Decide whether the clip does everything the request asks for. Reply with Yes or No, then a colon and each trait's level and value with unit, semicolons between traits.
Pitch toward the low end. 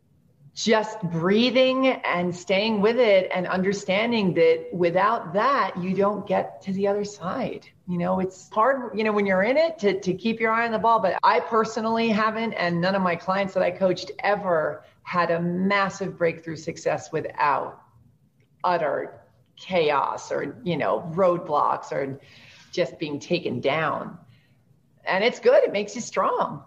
No: high, 190 Hz